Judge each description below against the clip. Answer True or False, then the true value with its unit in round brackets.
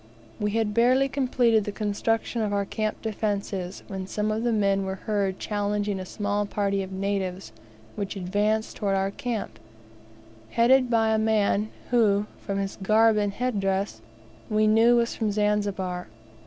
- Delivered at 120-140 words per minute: False (160 wpm)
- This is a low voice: False (210 Hz)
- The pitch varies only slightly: True (2.0 semitones)